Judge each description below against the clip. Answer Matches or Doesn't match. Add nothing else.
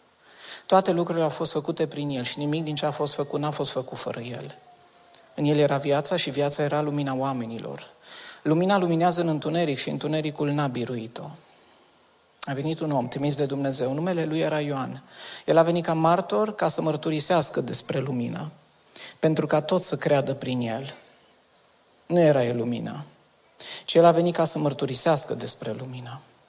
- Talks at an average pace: Doesn't match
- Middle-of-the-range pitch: Matches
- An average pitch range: Matches